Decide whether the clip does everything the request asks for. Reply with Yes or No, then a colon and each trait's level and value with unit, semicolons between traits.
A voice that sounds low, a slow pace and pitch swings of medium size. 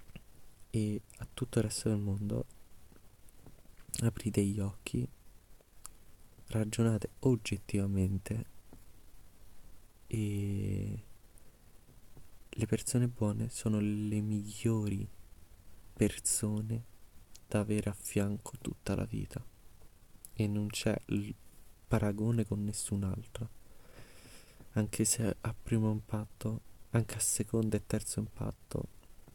No: low, 105 Hz; slow, 95 wpm; narrow, 2.0 semitones